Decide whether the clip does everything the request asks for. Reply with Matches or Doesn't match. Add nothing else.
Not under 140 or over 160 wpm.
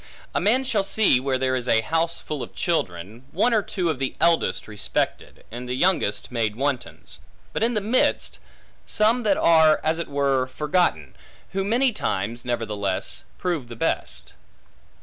Doesn't match